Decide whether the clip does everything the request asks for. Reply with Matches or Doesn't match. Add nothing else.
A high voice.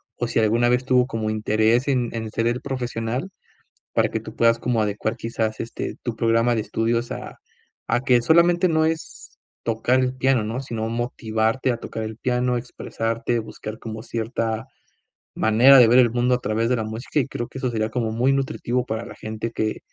Doesn't match